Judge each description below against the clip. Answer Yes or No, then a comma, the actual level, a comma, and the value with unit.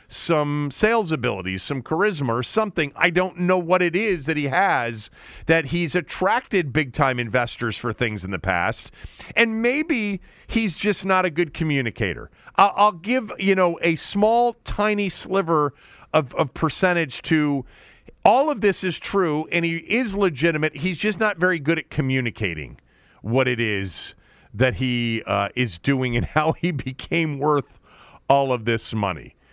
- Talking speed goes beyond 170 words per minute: No, average, 165 wpm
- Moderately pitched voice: Yes, medium, 160 Hz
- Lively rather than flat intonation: Yes, wide, 7.1 semitones